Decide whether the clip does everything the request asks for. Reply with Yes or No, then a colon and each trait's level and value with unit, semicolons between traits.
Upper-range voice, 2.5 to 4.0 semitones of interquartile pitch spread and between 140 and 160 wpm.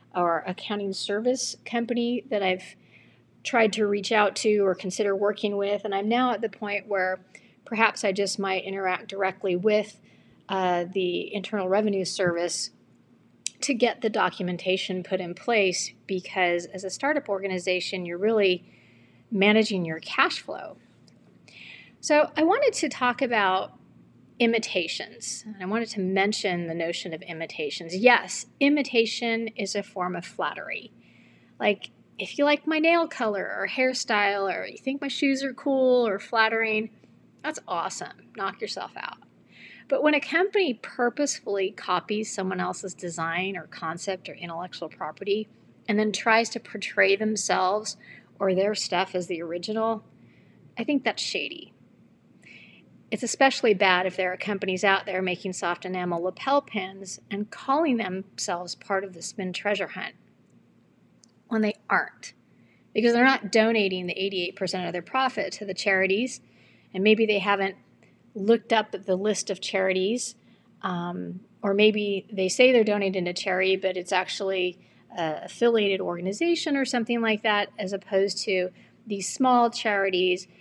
Yes: high, 200 Hz; average, 3.5 semitones; average, 150 wpm